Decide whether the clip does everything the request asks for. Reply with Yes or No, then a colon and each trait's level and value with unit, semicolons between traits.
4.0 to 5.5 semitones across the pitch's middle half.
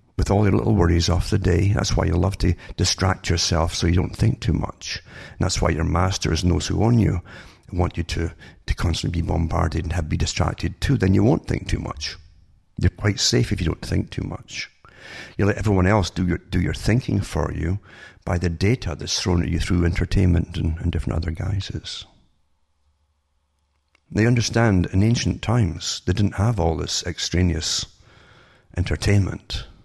No: average, 3.2 semitones